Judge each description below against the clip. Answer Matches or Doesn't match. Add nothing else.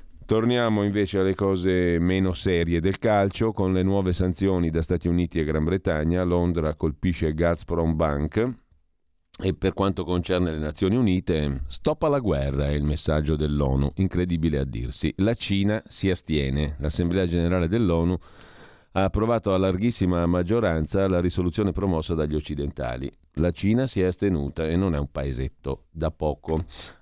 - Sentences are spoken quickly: Doesn't match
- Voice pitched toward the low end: Matches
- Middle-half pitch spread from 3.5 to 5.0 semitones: Matches